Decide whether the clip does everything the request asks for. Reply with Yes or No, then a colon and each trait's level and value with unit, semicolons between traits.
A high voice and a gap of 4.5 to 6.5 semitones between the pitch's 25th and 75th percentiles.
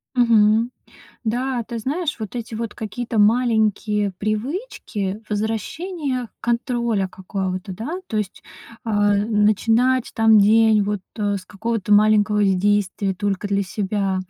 No: high, 215 Hz; narrow, 2.4 semitones